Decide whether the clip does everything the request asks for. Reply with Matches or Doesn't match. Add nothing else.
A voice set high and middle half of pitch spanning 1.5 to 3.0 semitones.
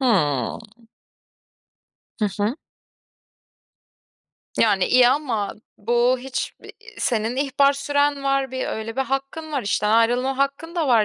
Doesn't match